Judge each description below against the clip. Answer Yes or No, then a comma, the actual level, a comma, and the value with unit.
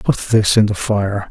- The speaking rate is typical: No, fast, 230 wpm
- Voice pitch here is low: Yes, low, 105 Hz